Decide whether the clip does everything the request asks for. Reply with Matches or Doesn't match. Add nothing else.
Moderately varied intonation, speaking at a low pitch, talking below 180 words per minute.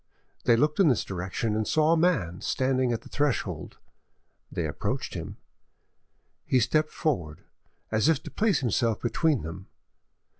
Doesn't match